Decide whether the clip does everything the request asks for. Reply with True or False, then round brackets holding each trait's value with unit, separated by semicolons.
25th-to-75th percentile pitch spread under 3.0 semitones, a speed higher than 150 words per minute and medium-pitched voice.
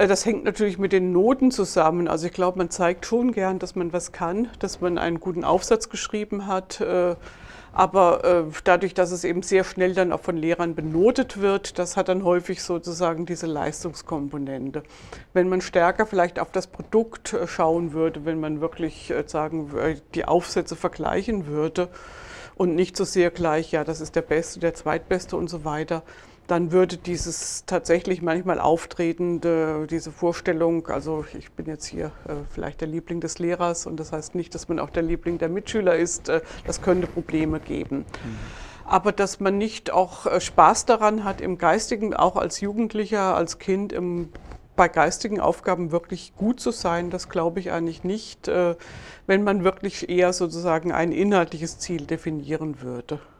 True (2.5 semitones; 165 wpm; 175 Hz)